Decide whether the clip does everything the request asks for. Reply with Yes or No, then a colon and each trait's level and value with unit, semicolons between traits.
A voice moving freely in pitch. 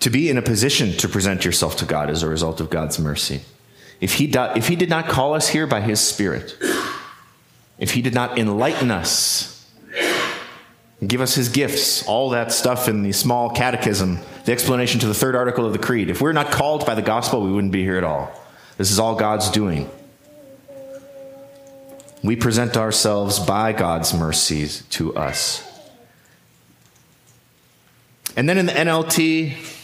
Yes: wide, 6.9 semitones